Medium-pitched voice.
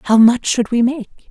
No: high, 240 Hz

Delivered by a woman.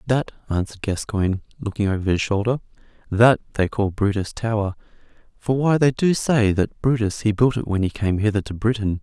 No: male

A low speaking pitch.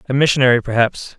Yes: low, 130 Hz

